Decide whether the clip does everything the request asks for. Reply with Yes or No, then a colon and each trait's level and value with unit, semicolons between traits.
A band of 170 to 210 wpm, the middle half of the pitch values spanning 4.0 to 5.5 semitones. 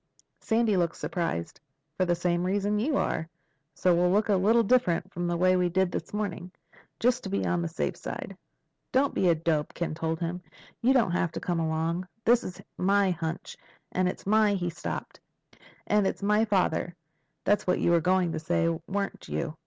No: average, 190 wpm; average, 3.1 semitones